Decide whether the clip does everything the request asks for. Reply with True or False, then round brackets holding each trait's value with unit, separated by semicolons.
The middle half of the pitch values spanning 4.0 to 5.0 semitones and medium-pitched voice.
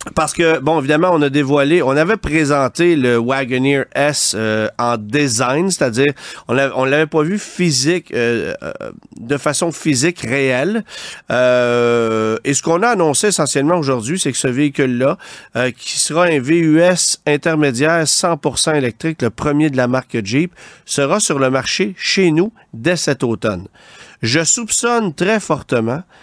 True (4.5 semitones; 150 Hz)